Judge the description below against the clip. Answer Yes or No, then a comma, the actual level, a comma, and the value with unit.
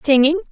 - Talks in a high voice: Yes, very high, 300 Hz